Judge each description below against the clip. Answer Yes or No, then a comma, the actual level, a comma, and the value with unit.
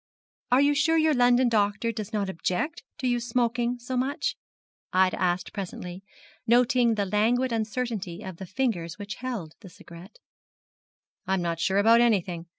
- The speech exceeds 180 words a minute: No, average, 160 wpm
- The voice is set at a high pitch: Yes, high, 220 Hz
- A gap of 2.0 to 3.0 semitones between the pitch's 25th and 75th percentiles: No, average, 4.6 semitones